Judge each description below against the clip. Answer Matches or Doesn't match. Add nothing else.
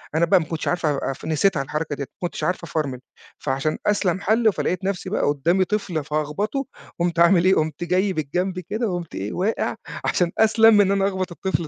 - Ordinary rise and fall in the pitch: Matches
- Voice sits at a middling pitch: Matches